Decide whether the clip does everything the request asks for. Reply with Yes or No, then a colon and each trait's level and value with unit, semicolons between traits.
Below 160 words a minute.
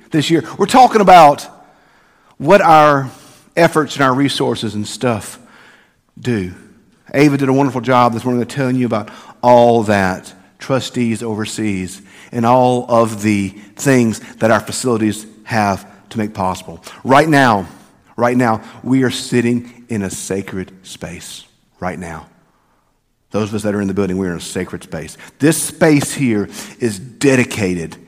Yes: average, 150 wpm